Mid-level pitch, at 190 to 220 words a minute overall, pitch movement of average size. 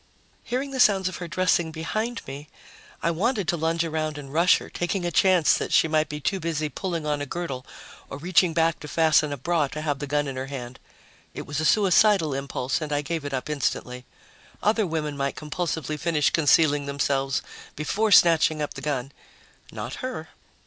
Yes: medium, 155 Hz; average, 195 wpm; average, 3.3 semitones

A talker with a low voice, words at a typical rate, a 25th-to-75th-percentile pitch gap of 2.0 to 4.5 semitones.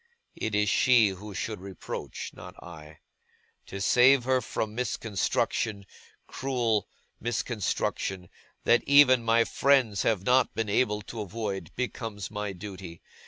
No: low, 110 Hz; slow, 125 wpm; average, 3.7 semitones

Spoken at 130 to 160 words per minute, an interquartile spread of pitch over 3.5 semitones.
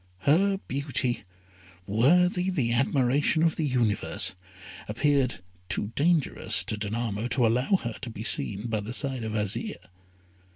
Yes: slow, 135 wpm; average, 4.8 semitones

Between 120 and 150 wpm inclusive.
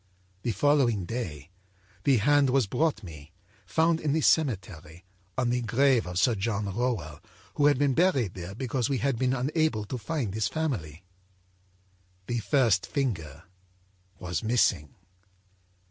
Yes: average, 145 wpm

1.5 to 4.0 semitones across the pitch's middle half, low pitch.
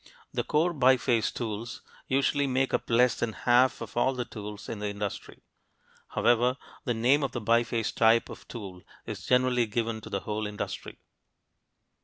Yes: average, 2.7 semitones; low, 120 Hz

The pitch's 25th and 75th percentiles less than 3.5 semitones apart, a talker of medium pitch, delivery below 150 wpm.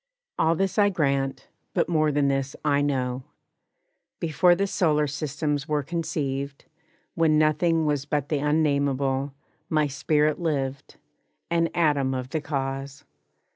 Yes: narrow, 2.5 semitones; medium, 150 Hz; slow, 135 wpm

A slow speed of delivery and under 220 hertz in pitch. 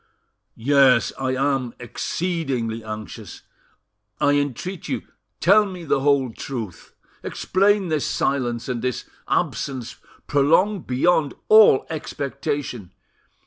Yes: slow, 100 wpm; medium, 140 Hz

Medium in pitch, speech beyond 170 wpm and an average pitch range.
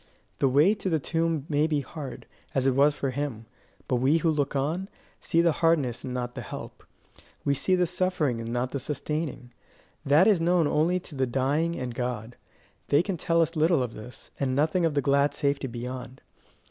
Yes: medium, 145 Hz; average, 200 wpm; average, 4.2 semitones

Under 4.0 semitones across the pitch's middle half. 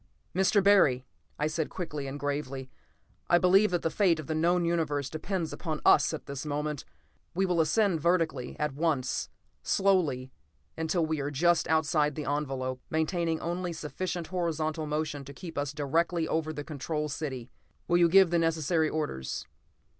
Yes: average, 2.9 semitones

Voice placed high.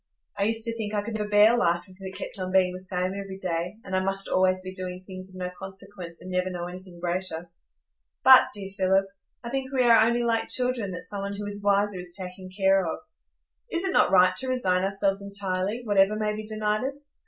Yes: high, 195 Hz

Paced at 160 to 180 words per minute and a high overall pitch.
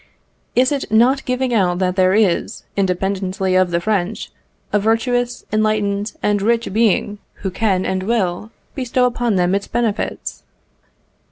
No: average, 145 wpm; high, 210 Hz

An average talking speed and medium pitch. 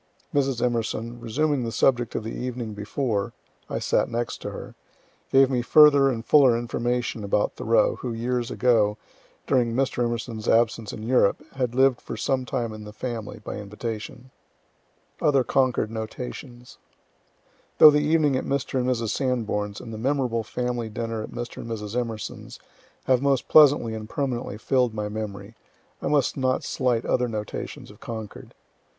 No: average, 160 wpm; low, 120 Hz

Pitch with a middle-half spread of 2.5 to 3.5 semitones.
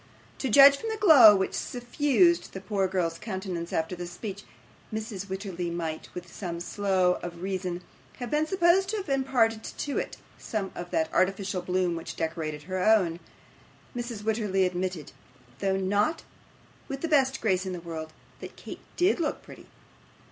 No: wide, 5.6 semitones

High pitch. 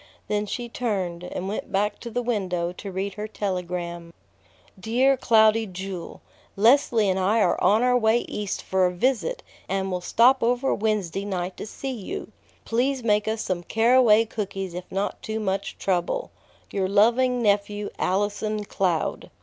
Yes: high, 205 Hz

